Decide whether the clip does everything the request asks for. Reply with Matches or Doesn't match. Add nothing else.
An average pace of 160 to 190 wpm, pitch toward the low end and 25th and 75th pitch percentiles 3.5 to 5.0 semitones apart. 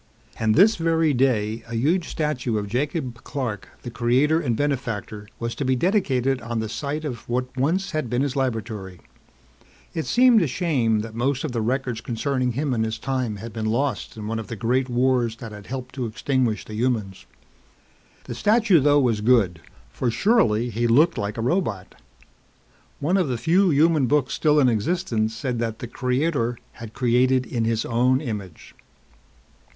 Matches